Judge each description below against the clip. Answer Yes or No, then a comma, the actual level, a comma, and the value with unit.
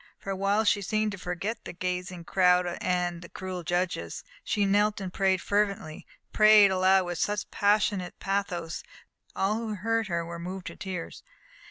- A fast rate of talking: No, average, 175 wpm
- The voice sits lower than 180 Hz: No, high, 190 Hz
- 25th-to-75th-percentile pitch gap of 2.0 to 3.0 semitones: Yes, narrow, 2.5 semitones